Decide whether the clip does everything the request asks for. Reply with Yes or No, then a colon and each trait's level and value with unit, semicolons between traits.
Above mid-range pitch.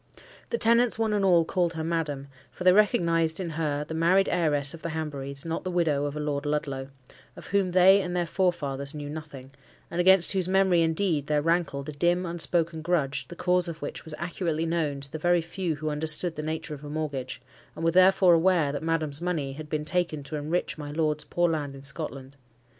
No: medium, 160 Hz